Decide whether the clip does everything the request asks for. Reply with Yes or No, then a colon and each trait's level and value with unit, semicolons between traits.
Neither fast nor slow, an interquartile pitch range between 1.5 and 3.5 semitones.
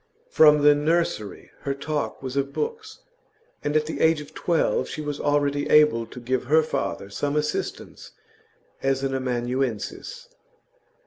Yes: average, 145 wpm; narrow, 2.6 semitones